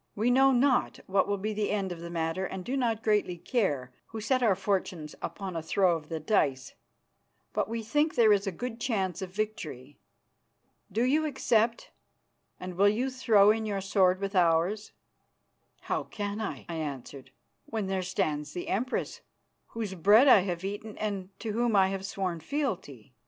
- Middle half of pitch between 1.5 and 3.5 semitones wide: No, average, 3.9 semitones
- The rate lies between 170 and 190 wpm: Yes, average, 180 wpm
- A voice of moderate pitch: No, high, 200 Hz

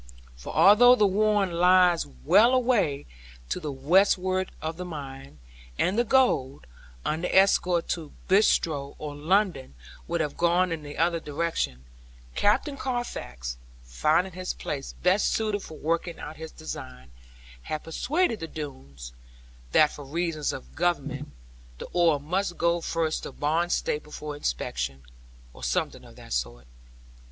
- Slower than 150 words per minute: Yes, average, 140 wpm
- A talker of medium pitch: Yes, medium, 165 Hz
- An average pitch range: Yes, average, 4.5 semitones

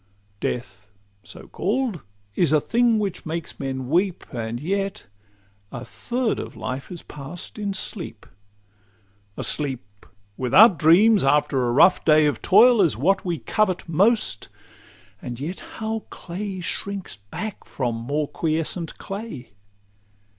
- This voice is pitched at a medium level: Yes, medium, 170 Hz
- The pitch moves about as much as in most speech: No, wide, 7.0 semitones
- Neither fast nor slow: No, slow, 130 wpm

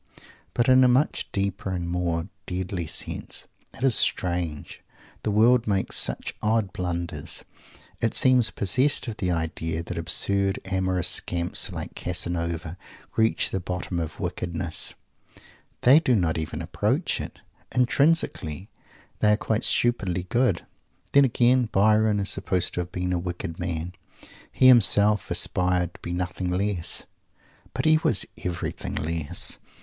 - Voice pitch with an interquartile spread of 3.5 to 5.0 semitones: Yes, average, 4.3 semitones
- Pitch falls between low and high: No, very low, 95 Hz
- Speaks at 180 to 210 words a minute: No, average, 140 wpm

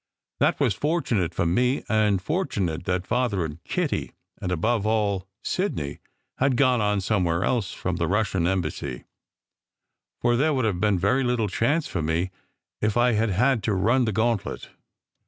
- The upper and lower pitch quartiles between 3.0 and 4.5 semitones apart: No, average, 5.0 semitones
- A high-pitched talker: No, low, 105 Hz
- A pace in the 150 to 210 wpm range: Yes, average, 170 wpm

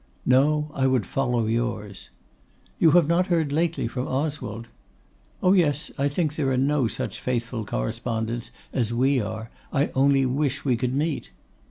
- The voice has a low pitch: Yes, low, 130 Hz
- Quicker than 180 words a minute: No, average, 160 wpm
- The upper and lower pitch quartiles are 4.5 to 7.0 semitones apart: No, average, 4.0 semitones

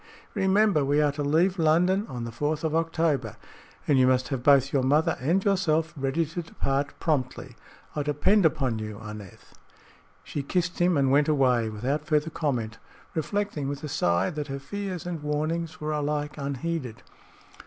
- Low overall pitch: No, medium, 150 Hz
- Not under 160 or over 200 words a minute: Yes, average, 170 wpm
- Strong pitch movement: No, average, 3.5 semitones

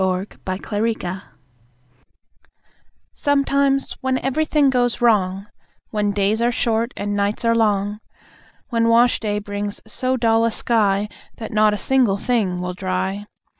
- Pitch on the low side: No, high, 215 Hz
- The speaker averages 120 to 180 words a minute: Yes, average, 140 wpm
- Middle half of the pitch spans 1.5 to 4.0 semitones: Yes, average, 3.1 semitones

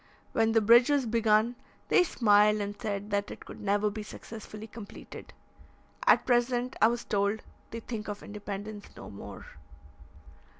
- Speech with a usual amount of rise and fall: No, narrow, 2.1 semitones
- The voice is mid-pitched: No, high, 215 Hz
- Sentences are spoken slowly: No, average, 155 wpm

